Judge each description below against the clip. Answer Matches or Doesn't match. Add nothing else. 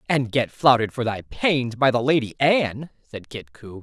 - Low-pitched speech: Matches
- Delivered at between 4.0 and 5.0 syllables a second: Matches